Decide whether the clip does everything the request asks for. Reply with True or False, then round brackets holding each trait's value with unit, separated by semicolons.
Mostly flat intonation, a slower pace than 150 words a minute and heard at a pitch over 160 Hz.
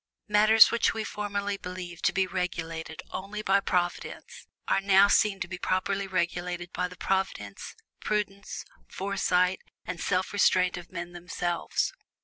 True (2.1 semitones; 140 wpm; 185 Hz)